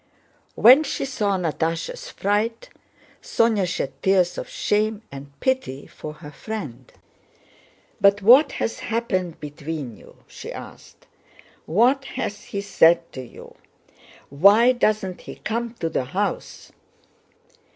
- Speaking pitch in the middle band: No, high, 200 Hz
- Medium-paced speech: No, slow, 120 wpm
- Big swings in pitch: Yes, wide, 6.2 semitones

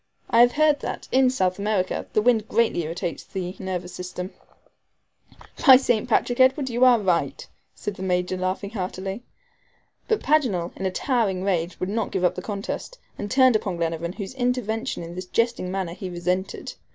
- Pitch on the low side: No, high, 195 Hz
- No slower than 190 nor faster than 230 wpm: No, average, 175 wpm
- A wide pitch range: No, average, 4.8 semitones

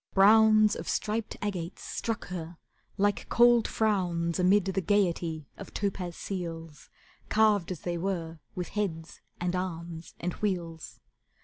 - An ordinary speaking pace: No, slow, 130 wpm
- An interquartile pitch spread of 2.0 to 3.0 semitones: No, average, 3.5 semitones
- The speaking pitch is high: No, medium, 180 Hz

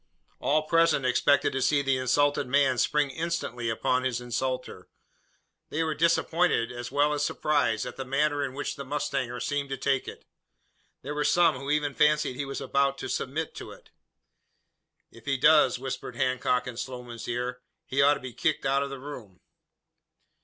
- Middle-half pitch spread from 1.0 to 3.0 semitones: Yes, average, 2.7 semitones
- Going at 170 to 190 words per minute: Yes, average, 180 wpm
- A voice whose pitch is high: No, medium, 140 Hz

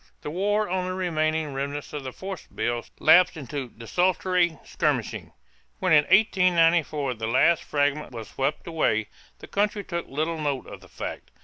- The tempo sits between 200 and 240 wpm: No, average, 165 wpm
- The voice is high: No, medium, 155 Hz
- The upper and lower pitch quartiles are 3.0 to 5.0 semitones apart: Yes, average, 4.6 semitones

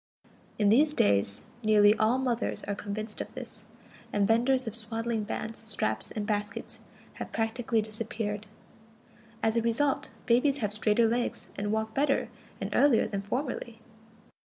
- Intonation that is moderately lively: No, narrow, 2.2 semitones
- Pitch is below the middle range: No, high, 225 Hz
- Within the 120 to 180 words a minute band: Yes, average, 145 wpm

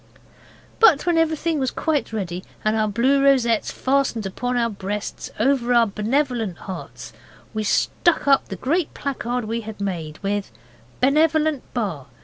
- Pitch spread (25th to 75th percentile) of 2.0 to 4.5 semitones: No, average, 5.0 semitones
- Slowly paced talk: No, average, 145 wpm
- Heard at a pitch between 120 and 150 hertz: No, high, 240 Hz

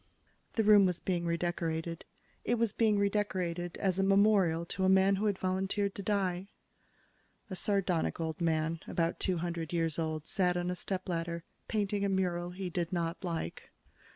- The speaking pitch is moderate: Yes, medium, 180 Hz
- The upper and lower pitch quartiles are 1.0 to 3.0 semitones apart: Yes, narrow, 2.6 semitones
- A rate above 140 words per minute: Yes, average, 170 wpm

